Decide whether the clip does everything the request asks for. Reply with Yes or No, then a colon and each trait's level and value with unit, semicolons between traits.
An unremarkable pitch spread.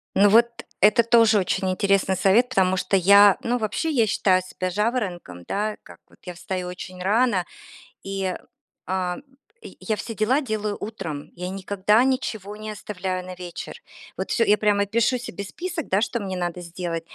Yes: average, 3.0 semitones